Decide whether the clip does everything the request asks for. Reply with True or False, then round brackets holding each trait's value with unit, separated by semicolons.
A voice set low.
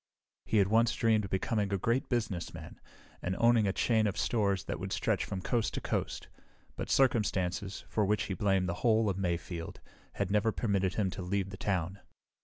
True (100 Hz)